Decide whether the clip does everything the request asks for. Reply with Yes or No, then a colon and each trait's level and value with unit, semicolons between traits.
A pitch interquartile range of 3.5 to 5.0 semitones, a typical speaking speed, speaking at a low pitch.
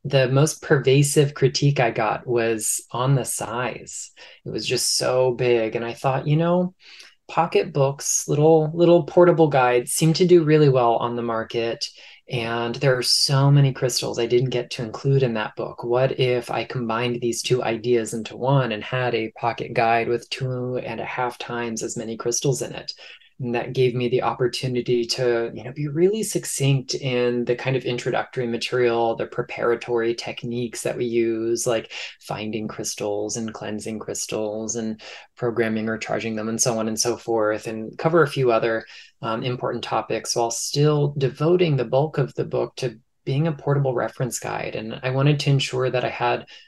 No: average, 3.0 semitones; average, 185 wpm; low, 125 Hz